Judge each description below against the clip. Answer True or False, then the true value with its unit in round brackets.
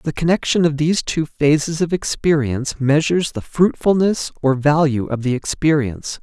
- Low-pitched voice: False (150 Hz)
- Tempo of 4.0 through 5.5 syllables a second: True (5.2 syllables/s)